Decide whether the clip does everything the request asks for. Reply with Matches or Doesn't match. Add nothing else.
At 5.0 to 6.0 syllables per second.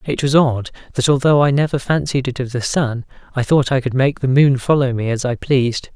Matches